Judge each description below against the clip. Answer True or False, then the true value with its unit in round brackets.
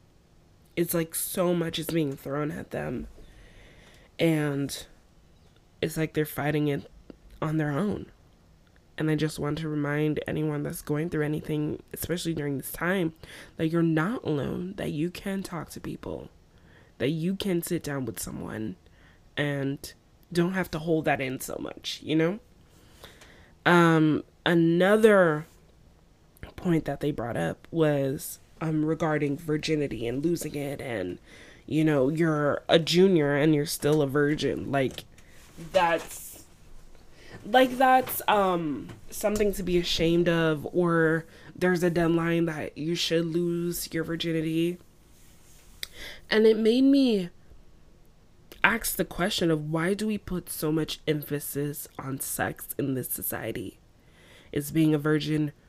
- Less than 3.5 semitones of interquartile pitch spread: True (2.8 semitones)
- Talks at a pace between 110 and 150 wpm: True (140 wpm)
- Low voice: False (155 Hz)